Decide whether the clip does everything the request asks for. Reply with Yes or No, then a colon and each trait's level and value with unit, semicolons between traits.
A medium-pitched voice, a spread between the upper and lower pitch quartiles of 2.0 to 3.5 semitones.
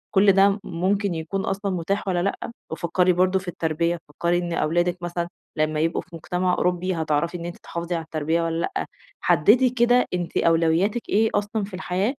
Yes: medium, 180 Hz; average, 2.8 semitones